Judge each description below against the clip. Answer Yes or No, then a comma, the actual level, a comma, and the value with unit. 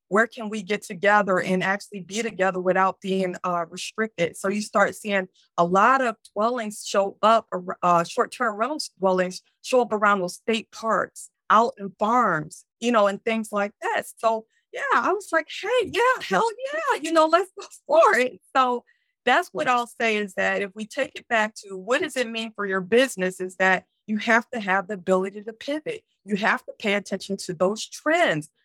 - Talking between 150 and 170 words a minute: No, fast, 205 wpm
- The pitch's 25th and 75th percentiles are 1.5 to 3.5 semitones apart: No, average, 4.1 semitones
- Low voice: No, high, 215 Hz